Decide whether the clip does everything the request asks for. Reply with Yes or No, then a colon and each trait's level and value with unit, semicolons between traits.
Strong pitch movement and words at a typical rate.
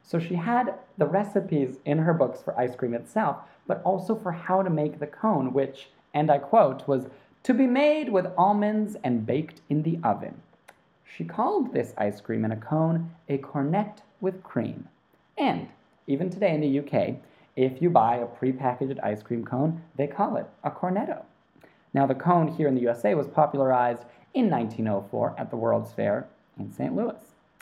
Yes: wide, 6.4 semitones; average, 185 wpm